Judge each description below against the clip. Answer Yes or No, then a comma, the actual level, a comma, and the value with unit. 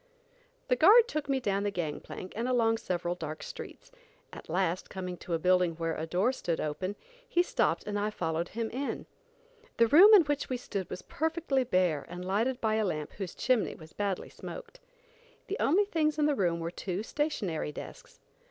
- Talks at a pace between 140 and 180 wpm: No, average, 195 wpm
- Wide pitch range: Yes, wide, 7.6 semitones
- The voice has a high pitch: Yes, high, 205 Hz